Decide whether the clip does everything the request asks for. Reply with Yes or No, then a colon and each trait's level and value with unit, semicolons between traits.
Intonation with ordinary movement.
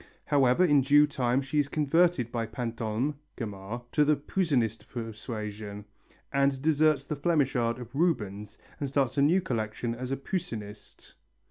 Yes: average, 4.6 semitones